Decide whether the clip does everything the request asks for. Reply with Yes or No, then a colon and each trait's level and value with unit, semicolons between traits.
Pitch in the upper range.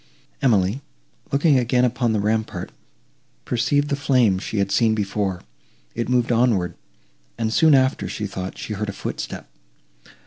No: low, 115 Hz